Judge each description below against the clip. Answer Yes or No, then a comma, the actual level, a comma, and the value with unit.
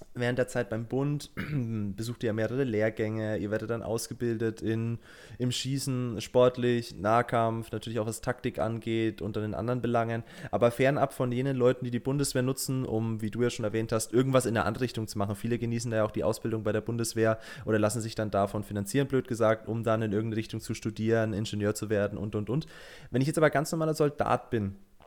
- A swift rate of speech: Yes, fast, 215 wpm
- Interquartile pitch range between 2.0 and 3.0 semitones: Yes, narrow, 2.4 semitones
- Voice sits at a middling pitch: No, low, 115 Hz